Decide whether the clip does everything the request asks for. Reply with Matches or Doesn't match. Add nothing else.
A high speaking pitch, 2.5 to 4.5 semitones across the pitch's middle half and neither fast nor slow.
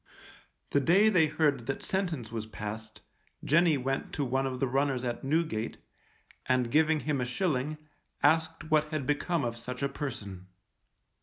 Doesn't match